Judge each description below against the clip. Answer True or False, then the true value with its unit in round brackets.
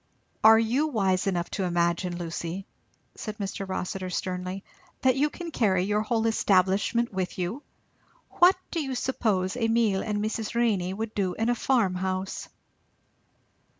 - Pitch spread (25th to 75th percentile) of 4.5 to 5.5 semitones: False (3.9 semitones)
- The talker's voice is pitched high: True (200 Hz)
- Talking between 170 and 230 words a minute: False (145 wpm)